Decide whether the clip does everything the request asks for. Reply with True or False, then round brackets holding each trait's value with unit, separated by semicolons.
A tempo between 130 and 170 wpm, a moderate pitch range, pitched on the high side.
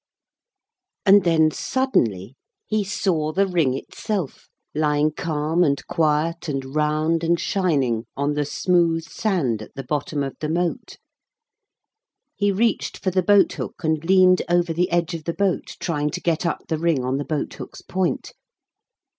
False (160 wpm; 3.5 semitones; 165 Hz)